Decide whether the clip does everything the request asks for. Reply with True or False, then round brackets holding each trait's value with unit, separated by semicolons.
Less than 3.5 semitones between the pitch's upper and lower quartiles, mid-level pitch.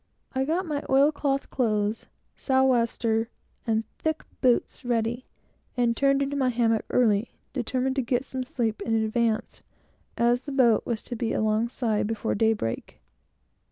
False (2.9 semitones; 240 Hz)